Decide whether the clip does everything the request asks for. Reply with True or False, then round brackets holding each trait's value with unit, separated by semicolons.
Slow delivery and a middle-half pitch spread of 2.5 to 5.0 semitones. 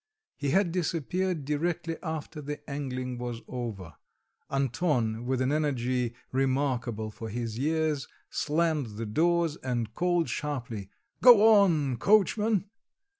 False (120 wpm; 5.4 semitones)